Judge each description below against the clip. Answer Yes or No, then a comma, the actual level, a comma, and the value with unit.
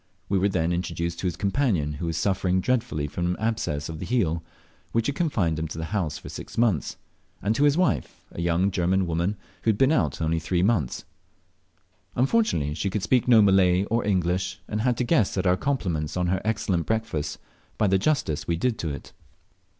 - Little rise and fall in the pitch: No, average, 5.1 semitones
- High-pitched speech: No, very low, 95 Hz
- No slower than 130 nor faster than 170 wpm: No, fast, 205 wpm